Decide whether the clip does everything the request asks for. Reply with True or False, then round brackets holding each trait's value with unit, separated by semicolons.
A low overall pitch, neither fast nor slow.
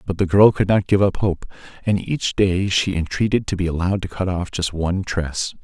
False (95 Hz; 235 wpm)